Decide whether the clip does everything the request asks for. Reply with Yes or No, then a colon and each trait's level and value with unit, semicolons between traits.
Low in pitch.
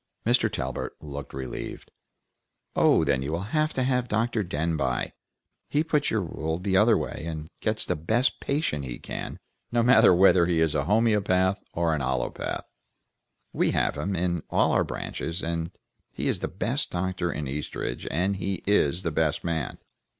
Yes: very low, 90 Hz